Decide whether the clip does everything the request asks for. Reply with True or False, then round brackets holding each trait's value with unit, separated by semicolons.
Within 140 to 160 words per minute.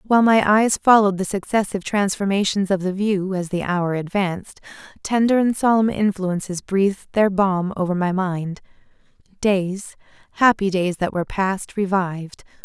True (145 wpm)